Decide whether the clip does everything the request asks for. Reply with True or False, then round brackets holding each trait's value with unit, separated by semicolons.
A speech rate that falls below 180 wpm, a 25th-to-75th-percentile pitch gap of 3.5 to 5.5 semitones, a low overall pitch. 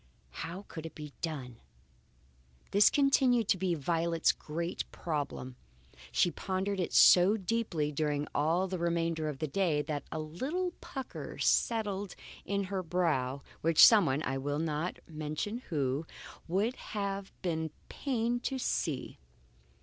False (135 wpm; 4.7 semitones; 170 Hz)